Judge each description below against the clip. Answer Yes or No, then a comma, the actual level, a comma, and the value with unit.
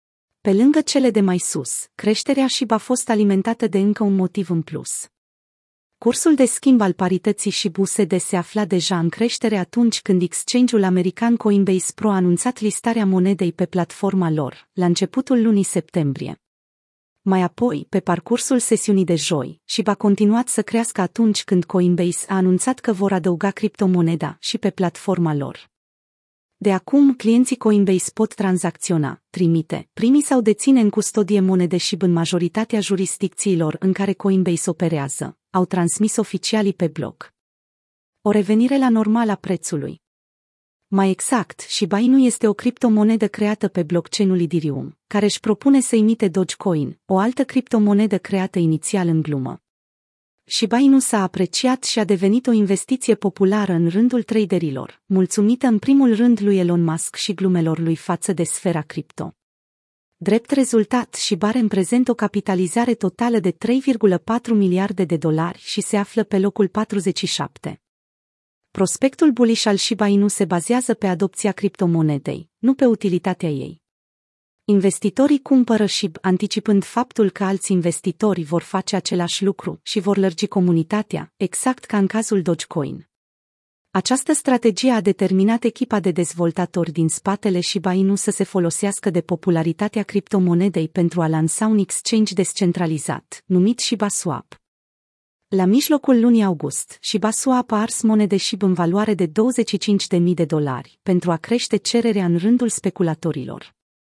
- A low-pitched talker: No, high, 200 Hz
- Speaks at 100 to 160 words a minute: Yes, average, 145 wpm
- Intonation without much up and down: No, average, 3.8 semitones